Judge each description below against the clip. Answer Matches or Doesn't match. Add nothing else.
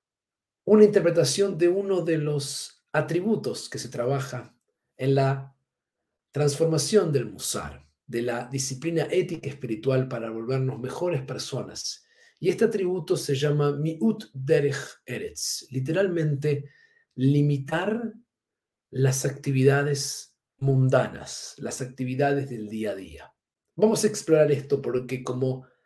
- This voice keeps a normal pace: Doesn't match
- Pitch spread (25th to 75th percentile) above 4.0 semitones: Matches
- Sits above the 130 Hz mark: Matches